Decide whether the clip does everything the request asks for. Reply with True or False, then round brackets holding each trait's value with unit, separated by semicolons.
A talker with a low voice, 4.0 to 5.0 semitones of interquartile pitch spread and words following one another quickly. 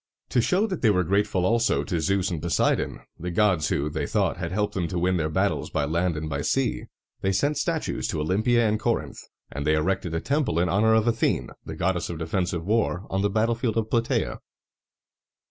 True (95 Hz; 4.7 semitones; 210 wpm)